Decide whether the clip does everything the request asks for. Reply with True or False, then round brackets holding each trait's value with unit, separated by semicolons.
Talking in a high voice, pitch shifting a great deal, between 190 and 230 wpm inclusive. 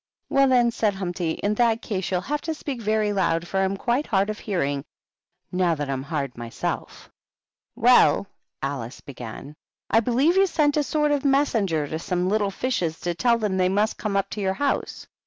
True (200 Hz; 6.1 semitones; 195 wpm)